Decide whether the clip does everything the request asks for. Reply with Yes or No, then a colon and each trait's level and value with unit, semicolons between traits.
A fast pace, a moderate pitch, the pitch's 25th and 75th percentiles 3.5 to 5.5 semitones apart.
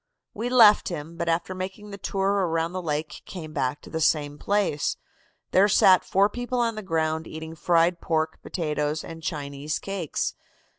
No: average, 170 wpm; medium, 165 Hz; average, 3.8 semitones